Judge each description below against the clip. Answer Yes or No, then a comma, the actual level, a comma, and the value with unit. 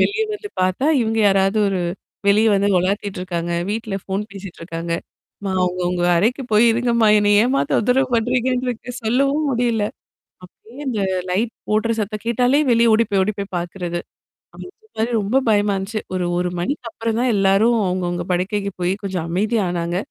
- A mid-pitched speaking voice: No, high, 210 Hz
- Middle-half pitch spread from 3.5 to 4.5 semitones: Yes, average, 4.0 semitones